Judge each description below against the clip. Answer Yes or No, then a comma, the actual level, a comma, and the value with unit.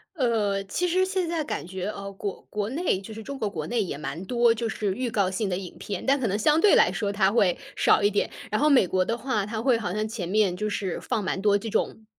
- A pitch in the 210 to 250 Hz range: Yes, high, 215 Hz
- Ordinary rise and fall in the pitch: Yes, average, 3.6 semitones